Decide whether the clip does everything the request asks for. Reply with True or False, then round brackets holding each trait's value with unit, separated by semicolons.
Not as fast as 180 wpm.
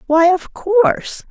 True (140 wpm)